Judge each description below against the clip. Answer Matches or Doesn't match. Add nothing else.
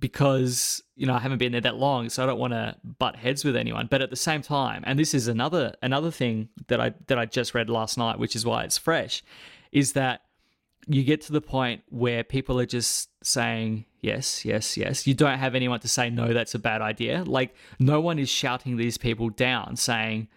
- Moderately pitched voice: Doesn't match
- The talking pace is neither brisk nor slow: Doesn't match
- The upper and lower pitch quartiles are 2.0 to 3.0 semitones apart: Matches